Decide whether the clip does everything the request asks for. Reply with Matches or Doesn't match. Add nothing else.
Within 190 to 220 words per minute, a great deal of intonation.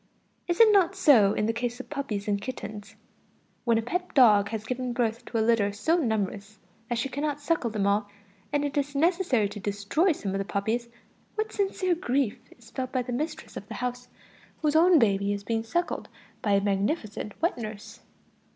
Matches